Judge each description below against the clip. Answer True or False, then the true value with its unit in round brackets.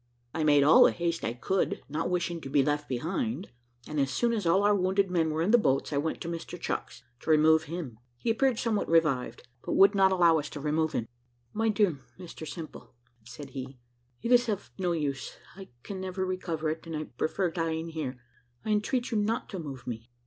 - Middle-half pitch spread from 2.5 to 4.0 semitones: False (4.6 semitones)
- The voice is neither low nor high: True (165 Hz)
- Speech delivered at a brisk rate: True (215 wpm)